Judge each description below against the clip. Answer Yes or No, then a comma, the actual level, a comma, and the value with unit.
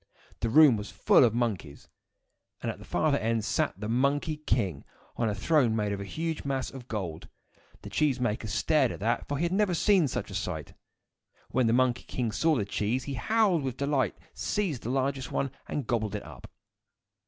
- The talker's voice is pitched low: Yes, low, 125 Hz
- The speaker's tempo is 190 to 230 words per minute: Yes, average, 200 wpm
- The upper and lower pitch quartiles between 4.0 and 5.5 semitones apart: Yes, average, 5.1 semitones